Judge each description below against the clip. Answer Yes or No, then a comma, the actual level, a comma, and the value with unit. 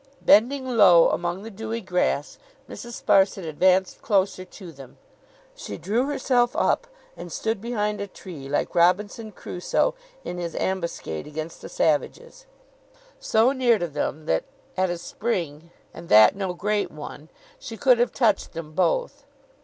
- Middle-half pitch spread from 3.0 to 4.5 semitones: No, average, 5.1 semitones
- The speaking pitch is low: No, high, 190 Hz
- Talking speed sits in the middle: Yes, average, 150 wpm